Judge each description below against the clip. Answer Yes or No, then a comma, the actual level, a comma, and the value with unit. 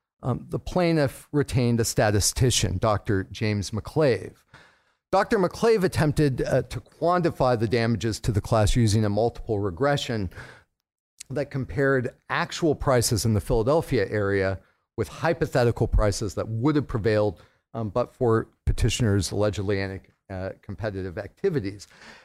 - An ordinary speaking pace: No, slow, 130 wpm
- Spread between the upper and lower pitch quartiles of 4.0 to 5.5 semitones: Yes, average, 5.0 semitones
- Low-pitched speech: Yes, low, 115 Hz